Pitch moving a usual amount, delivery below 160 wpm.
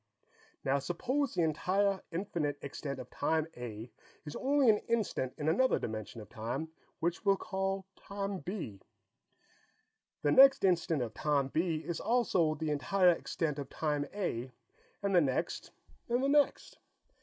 No: wide, 5.9 semitones; average, 150 wpm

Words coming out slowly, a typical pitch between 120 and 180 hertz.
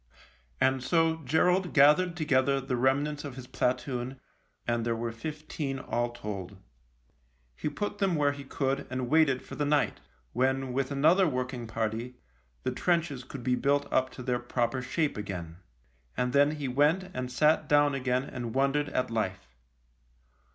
No: average, 165 wpm; low, 135 Hz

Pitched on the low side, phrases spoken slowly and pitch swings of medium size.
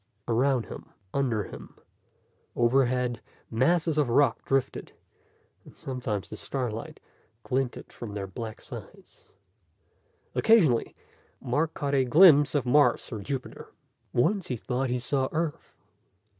Yes: low, 130 Hz; slow, 120 wpm; average, 3.3 semitones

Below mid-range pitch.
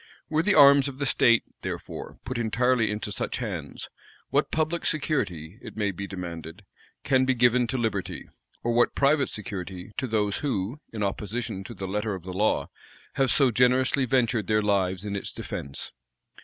Yes: low, 110 Hz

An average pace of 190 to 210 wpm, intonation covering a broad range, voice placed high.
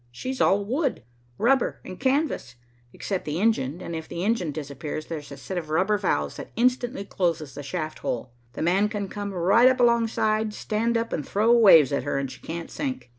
Yes: average, 200 wpm; wide, 6.8 semitones; high, 195 Hz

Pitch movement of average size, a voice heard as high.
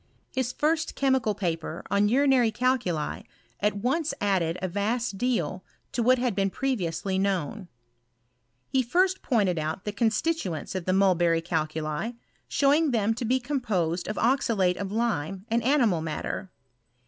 No: wide, 5.8 semitones; high, 210 Hz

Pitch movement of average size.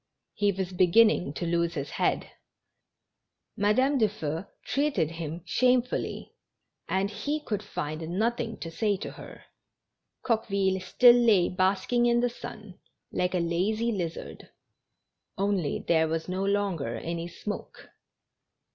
Yes: average, 4.7 semitones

